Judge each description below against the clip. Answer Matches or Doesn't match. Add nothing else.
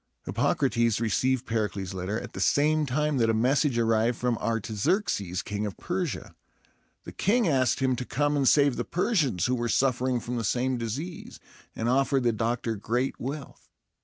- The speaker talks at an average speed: Matches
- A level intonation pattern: Doesn't match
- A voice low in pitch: Matches